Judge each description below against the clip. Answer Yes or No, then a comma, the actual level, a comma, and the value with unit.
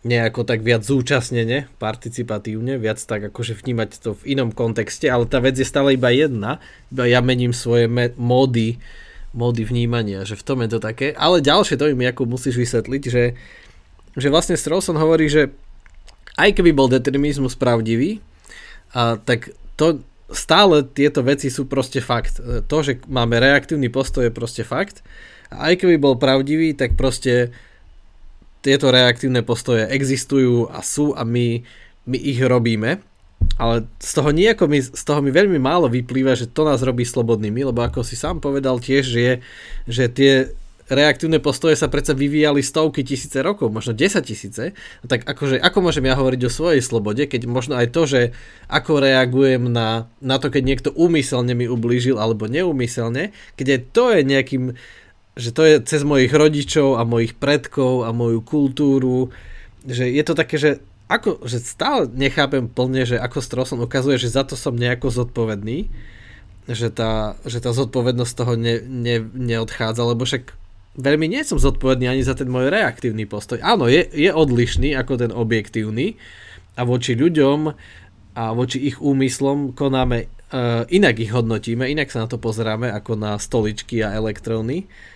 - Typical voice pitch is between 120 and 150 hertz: Yes, low, 125 Hz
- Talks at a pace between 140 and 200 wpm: Yes, fast, 165 wpm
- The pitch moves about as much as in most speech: Yes, average, 3.1 semitones